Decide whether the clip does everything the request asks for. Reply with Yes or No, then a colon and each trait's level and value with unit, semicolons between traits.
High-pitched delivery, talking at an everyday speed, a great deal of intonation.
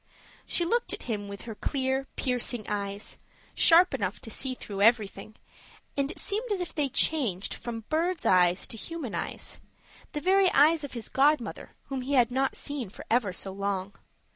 Yes: very high, 250 Hz; average, 180 wpm; wide, 6.6 semitones